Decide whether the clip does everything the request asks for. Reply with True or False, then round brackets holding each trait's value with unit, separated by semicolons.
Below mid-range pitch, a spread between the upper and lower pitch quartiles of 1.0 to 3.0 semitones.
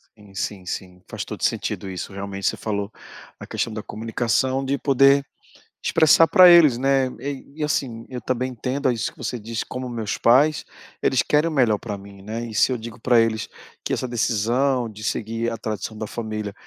False (115 Hz; 3.7 semitones)